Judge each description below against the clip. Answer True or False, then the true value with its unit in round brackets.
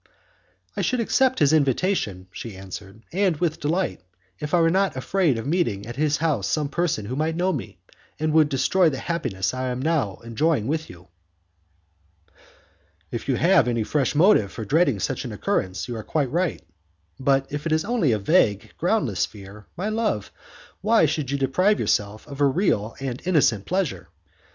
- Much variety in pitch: True (7.0 semitones)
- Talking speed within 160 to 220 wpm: True (180 wpm)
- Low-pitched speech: False (145 Hz)